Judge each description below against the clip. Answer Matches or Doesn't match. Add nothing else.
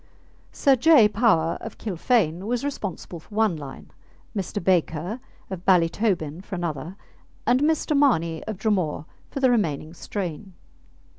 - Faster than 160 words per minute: Doesn't match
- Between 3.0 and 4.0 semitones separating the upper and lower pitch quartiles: Doesn't match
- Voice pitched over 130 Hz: Matches